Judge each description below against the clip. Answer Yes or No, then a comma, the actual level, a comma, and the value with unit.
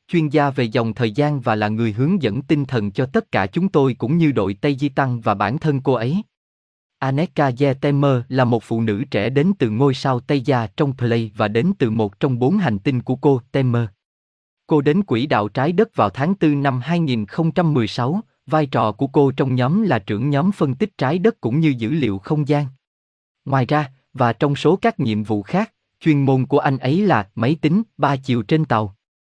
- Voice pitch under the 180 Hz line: Yes, medium, 140 Hz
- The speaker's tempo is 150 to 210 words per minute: No, average, 220 wpm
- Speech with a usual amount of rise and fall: Yes, average, 4.8 semitones